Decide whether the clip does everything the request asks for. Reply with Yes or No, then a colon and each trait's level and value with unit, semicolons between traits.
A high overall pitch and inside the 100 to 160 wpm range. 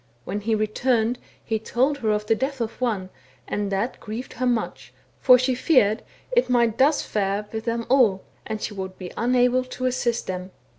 No: high, 230 Hz; average, 190 wpm